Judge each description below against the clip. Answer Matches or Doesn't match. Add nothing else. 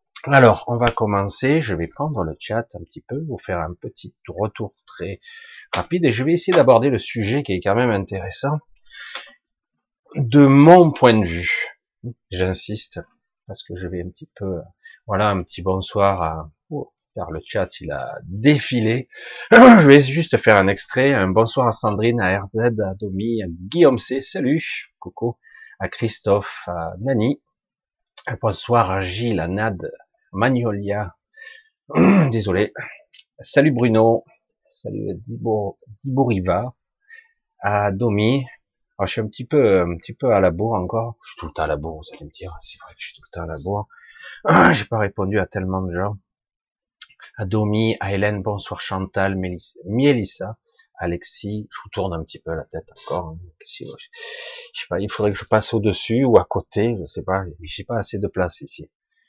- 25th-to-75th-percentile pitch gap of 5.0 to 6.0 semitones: Matches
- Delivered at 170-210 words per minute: Matches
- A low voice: Matches